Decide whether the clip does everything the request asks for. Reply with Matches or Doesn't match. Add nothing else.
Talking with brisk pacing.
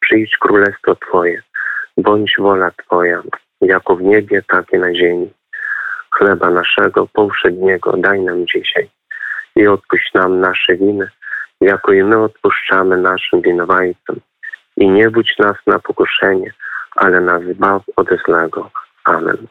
Doesn't match